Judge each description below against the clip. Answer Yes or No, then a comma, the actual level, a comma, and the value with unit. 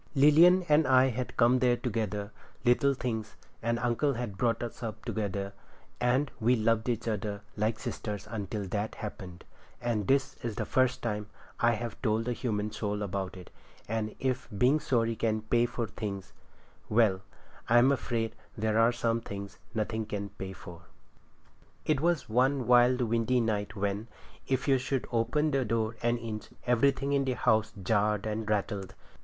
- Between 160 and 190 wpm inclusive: Yes, average, 165 wpm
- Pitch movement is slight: No, average, 3.0 semitones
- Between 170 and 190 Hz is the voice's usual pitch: No, low, 115 Hz